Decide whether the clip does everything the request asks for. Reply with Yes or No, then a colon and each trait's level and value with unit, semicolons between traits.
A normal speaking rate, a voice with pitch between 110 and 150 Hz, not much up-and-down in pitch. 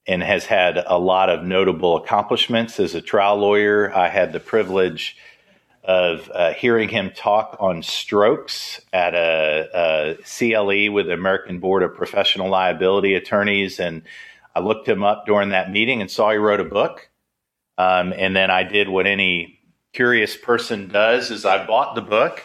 No: average, 170 wpm; very low, 95 Hz; narrow, 2.0 semitones